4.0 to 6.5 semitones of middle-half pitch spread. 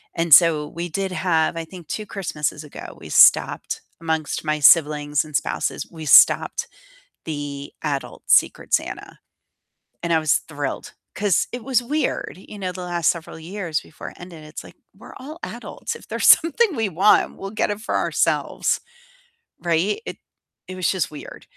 Yes: average, 4.3 semitones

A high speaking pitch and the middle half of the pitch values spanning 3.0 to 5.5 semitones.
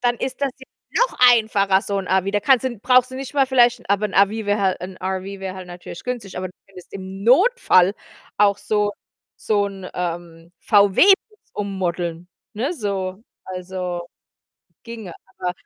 Yes: high, 200 Hz; average, 4.1 semitones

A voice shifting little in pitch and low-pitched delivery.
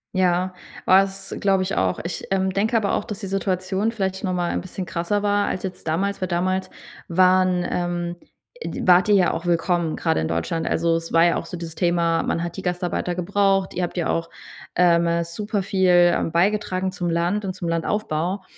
No: narrow, 2.1 semitones; medium, 180 Hz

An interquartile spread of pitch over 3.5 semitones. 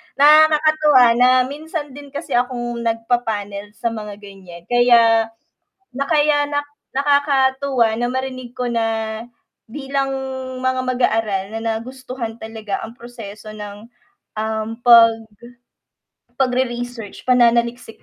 No: average, 3.1 semitones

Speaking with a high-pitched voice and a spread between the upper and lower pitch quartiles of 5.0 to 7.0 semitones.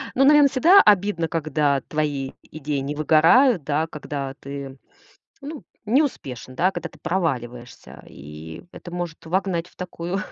No: medium, 160 Hz; wide, 5.5 semitones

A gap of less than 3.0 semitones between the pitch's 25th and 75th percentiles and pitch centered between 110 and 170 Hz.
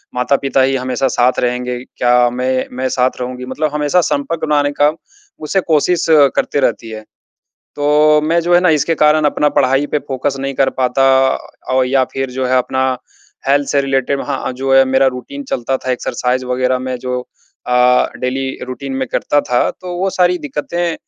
Yes: narrow, 2.6 semitones; low, 135 Hz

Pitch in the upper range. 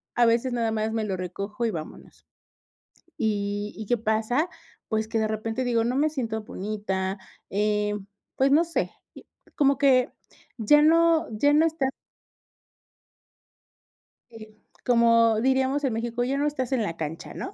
Yes: high, 230 Hz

